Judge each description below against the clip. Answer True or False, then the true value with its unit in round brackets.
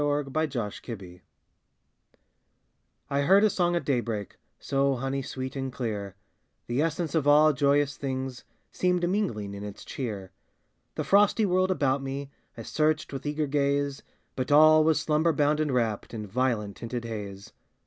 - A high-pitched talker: False (140 Hz)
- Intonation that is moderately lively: True (4.4 semitones)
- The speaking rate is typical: True (160 wpm)